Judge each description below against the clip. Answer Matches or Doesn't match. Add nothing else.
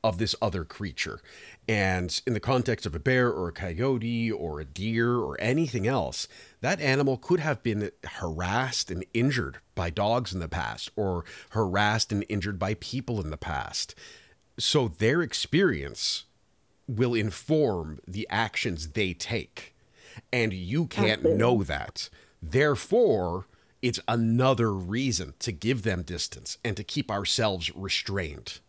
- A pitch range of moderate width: Matches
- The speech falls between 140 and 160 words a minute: Matches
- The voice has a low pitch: Matches